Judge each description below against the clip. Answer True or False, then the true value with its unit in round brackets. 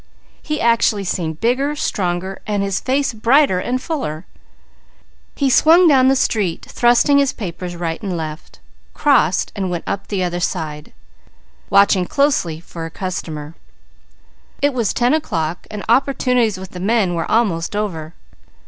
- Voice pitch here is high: True (200 Hz)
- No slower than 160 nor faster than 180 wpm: False (150 wpm)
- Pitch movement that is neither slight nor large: False (6.6 semitones)